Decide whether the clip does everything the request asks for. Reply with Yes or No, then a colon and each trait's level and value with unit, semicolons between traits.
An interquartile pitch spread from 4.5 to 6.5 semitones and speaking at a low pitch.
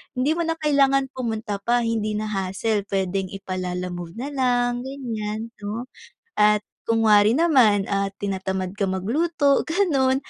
No: average, 5.1 semitones; high, 220 Hz